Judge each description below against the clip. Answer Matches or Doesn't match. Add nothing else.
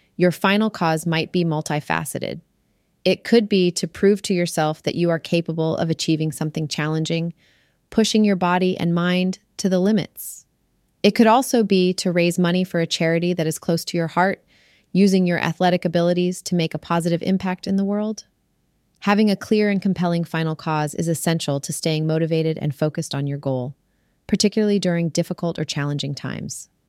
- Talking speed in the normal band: Matches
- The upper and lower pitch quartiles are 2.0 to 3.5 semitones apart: Matches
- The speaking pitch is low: Doesn't match